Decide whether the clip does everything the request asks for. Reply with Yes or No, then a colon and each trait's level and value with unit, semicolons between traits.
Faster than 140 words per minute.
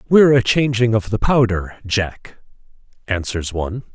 No: slow, 135 wpm